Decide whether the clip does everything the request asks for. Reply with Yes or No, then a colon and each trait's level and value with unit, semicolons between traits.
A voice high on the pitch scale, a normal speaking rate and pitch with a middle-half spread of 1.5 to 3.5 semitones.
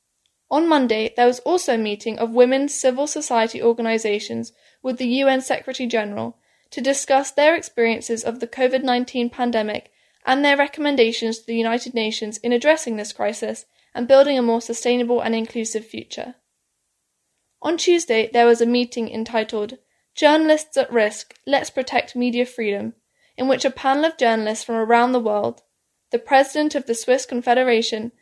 Yes: high, 245 Hz; average, 155 wpm; average, 2.9 semitones